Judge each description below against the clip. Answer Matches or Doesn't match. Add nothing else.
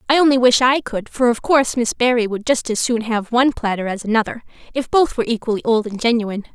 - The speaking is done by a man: Doesn't match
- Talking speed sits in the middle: Doesn't match